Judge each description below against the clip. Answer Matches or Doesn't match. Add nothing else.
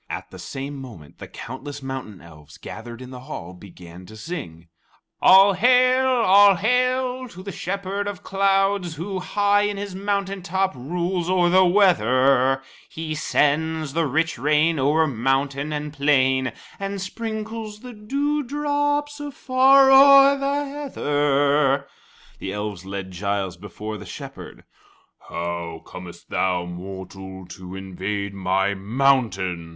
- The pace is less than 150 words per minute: Matches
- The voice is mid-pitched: Matches